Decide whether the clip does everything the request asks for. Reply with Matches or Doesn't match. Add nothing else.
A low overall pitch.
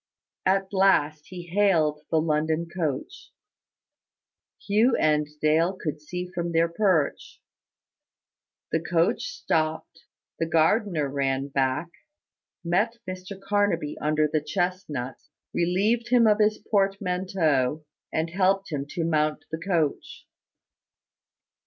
Doesn't match